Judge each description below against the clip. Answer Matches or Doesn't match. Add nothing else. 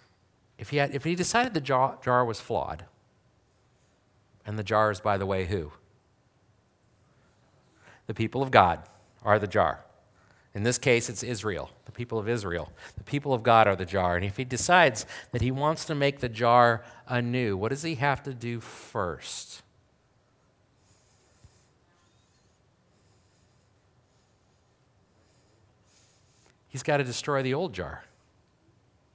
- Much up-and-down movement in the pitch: Doesn't match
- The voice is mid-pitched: Doesn't match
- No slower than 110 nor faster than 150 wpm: Matches